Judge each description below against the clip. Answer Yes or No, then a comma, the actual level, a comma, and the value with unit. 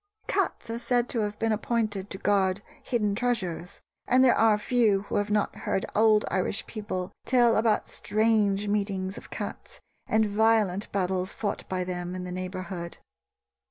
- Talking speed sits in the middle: Yes, average, 160 wpm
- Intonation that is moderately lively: Yes, average, 3.0 semitones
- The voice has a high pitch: Yes, high, 205 Hz